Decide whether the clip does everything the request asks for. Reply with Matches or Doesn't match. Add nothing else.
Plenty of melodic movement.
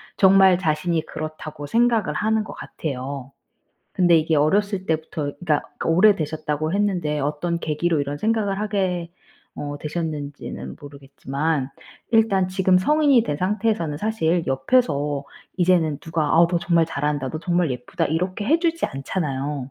Doesn't match